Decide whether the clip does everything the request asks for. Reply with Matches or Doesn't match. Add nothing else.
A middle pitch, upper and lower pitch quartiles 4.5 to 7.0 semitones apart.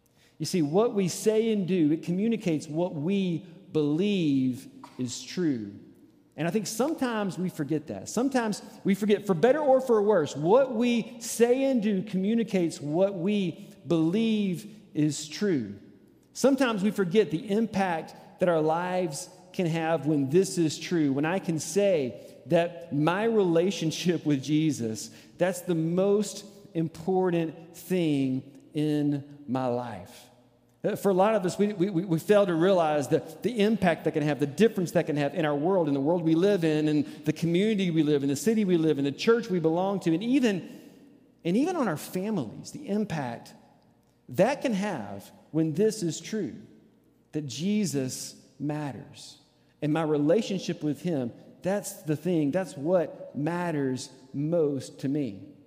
Matches